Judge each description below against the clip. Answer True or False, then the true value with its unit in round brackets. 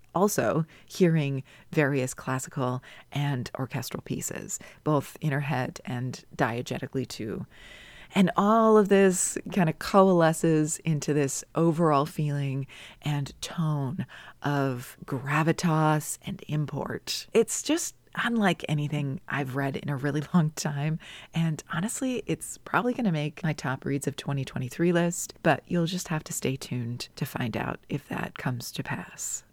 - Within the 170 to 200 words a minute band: False (140 wpm)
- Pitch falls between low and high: True (150 Hz)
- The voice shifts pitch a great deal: False (3.8 semitones)